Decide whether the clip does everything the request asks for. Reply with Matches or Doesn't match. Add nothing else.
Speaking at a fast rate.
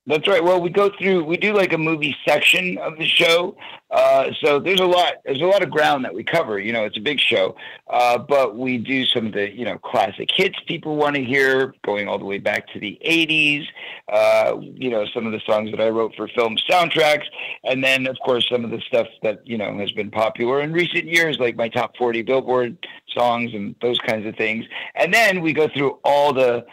Matches